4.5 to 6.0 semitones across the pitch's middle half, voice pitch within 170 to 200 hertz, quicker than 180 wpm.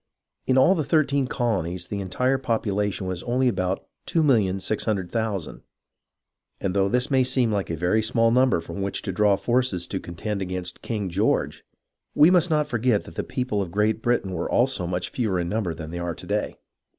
No: average, 5.2 semitones; low, 105 Hz; average, 190 wpm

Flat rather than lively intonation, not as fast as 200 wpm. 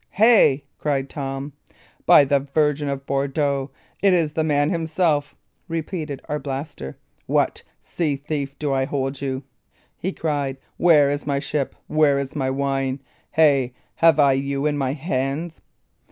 Yes: narrow, 2.1 semitones; average, 145 wpm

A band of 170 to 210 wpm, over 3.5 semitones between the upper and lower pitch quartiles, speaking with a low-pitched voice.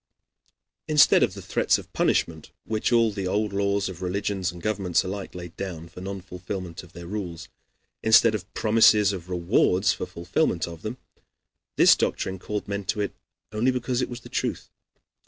No: average, 175 wpm; average, 3.0 semitones; low, 100 Hz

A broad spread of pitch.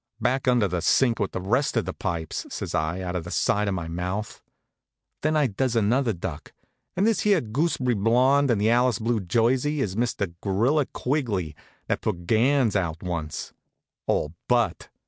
Yes: wide, 5.9 semitones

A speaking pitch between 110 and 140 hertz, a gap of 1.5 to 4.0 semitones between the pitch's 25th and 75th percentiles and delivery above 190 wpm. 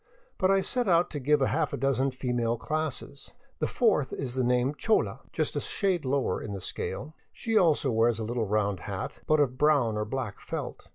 No: low, 135 Hz; average, 4.5 semitones; fast, 205 wpm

